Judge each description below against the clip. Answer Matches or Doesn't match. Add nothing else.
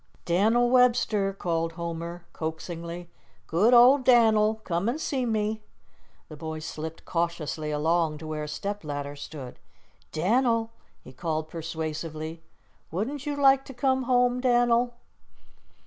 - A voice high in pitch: Doesn't match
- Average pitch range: Doesn't match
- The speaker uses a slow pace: Matches